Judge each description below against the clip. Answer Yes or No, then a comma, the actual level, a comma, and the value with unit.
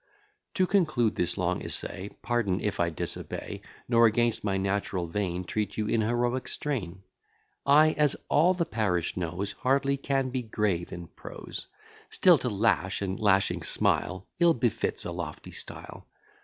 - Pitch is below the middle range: Yes, low, 110 Hz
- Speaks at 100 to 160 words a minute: Yes, average, 155 wpm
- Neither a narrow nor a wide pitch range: No, wide, 5.8 semitones